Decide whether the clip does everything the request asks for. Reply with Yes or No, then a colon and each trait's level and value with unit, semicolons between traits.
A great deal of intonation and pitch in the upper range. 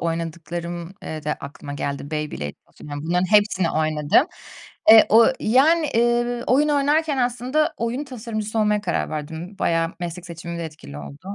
No: wide, 7.1 semitones; medium, 180 Hz